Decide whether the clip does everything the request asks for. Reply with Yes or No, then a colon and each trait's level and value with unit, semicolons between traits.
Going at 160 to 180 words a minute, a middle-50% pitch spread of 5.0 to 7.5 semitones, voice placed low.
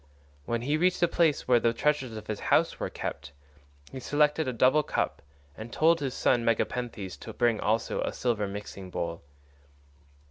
Yes: average, 175 wpm; average, 5.3 semitones; low, 120 Hz